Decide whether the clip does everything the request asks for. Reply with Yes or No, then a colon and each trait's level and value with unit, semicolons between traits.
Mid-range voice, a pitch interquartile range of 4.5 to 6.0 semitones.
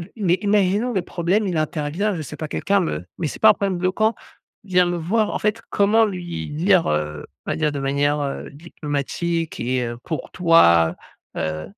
Yes: medium, 170 Hz; wide, 5.6 semitones